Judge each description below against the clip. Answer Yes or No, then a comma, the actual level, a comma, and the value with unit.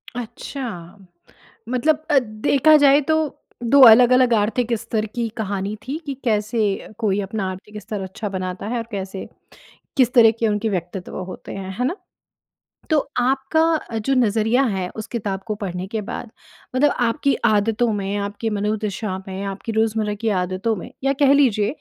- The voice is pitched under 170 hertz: No, high, 220 Hz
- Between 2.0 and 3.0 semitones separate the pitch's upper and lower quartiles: No, average, 3.9 semitones